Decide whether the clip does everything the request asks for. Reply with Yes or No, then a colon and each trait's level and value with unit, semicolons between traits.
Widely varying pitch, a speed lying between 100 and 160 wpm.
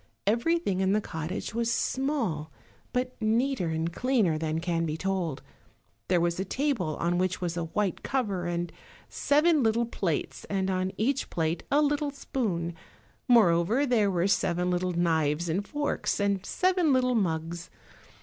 Yes: wide, 6.6 semitones; average, 155 wpm